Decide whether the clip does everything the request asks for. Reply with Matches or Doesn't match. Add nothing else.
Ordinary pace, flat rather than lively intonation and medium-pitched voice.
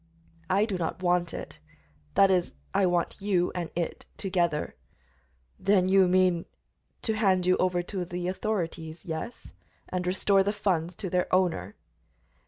Matches